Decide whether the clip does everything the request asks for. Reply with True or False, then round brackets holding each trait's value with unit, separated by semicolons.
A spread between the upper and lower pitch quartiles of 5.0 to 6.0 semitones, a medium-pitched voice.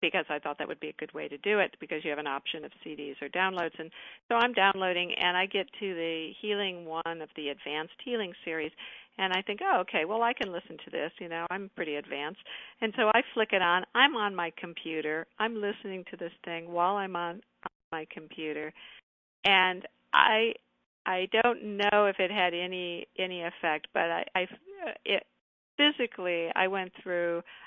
False (3.9 semitones; 180 Hz)